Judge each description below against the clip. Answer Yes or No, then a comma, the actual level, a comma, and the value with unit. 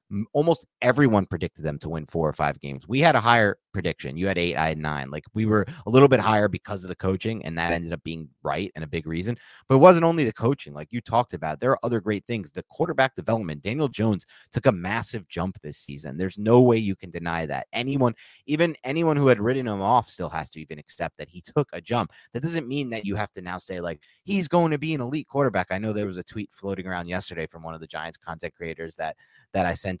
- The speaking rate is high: Yes, fast, 260 wpm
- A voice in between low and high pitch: No, low, 100 Hz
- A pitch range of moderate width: No, wide, 7.0 semitones